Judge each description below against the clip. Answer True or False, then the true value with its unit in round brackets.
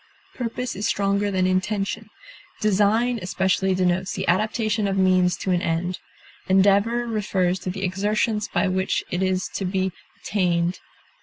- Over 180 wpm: False (145 wpm)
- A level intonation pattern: True (2.2 semitones)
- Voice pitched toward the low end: False (190 Hz)